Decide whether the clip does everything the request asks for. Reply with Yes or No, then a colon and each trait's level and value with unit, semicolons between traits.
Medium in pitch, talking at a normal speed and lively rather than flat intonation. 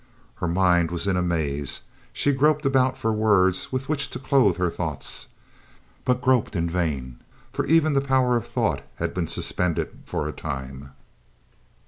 No: very low, 95 Hz; average, 165 wpm; wide, 7.8 semitones